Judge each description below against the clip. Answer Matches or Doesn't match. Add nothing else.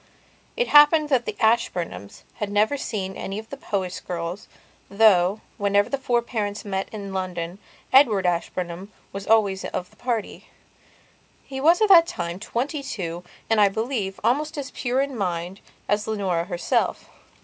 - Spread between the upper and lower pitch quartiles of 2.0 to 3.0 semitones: Doesn't match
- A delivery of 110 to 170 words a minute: Matches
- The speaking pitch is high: Matches